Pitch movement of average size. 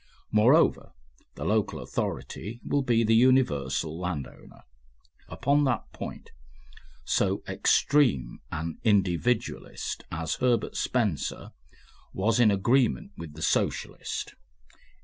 No: wide, 6.9 semitones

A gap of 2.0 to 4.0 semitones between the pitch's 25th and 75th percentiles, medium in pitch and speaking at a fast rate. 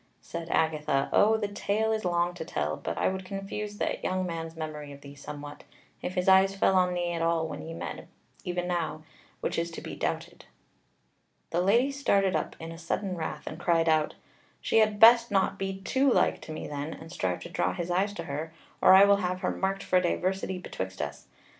Yes: average, 3.3 semitones; medium, 180 Hz; fast, 210 wpm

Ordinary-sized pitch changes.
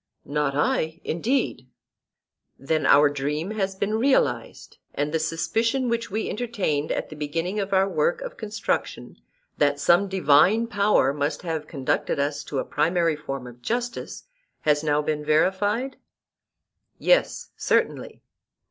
No: wide, 6.1 semitones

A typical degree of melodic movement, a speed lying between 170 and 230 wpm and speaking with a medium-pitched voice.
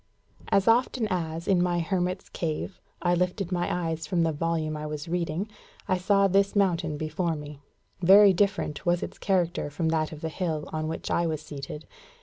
Yes: average, 3.0 semitones; average, 185 wpm; medium, 170 Hz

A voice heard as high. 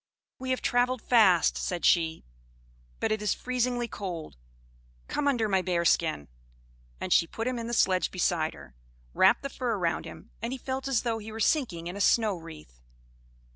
Yes: high, 215 Hz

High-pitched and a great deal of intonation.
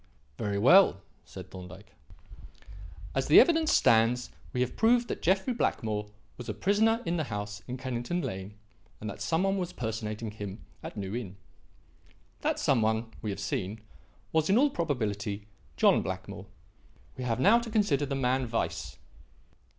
No: low, 125 Hz; wide, 8.8 semitones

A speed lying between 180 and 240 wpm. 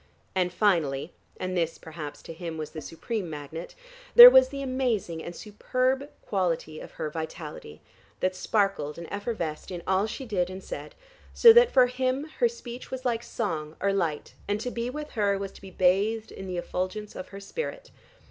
Yes: average, 185 wpm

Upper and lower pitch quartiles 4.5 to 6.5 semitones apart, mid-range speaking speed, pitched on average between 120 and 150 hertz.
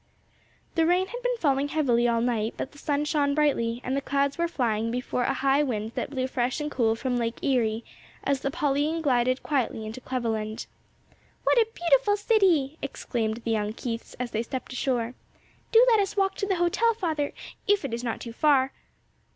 No: average, 5.0 semitones; average, 195 wpm; very high, 270 Hz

